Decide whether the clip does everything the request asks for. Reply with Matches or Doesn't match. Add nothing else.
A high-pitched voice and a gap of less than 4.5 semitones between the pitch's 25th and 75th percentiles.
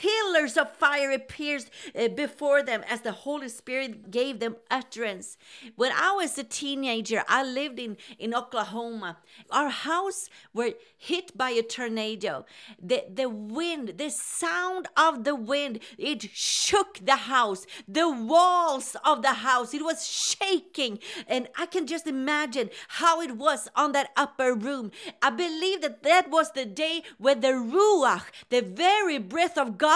Doesn't match